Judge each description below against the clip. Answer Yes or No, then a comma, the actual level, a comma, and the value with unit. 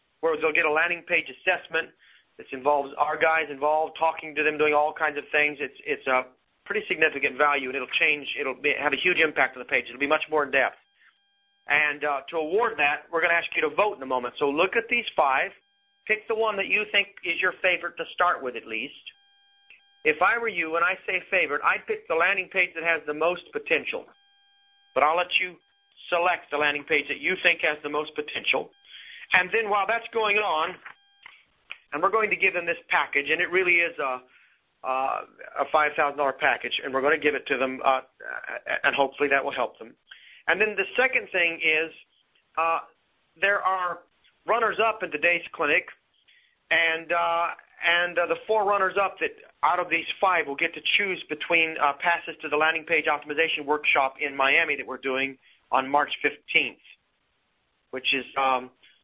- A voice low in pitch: No, medium, 165 Hz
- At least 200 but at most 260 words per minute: Yes, fast, 205 wpm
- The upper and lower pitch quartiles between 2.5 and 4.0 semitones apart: No, average, 4.8 semitones